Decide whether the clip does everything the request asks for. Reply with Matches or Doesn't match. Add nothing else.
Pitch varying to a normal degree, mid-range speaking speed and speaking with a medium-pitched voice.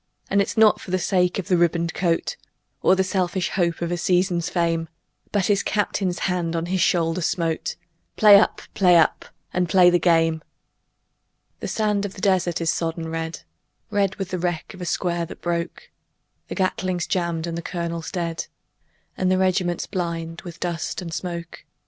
Doesn't match